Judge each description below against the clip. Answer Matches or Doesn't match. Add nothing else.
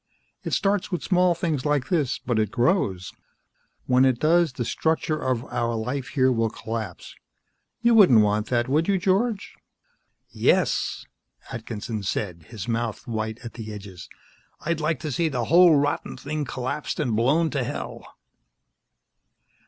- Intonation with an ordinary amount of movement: Doesn't match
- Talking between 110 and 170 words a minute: Matches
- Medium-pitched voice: Doesn't match